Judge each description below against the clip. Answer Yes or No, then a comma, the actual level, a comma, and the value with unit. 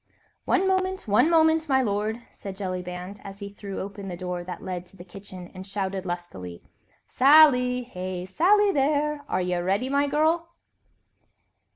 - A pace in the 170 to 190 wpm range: No, average, 160 wpm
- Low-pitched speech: No, high, 200 Hz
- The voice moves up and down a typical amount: No, wide, 8.0 semitones